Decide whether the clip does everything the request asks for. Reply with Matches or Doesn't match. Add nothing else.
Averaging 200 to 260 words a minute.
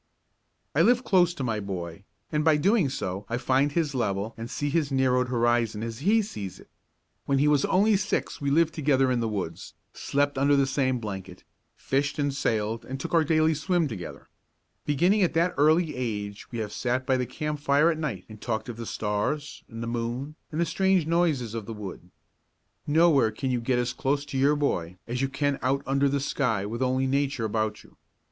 Matches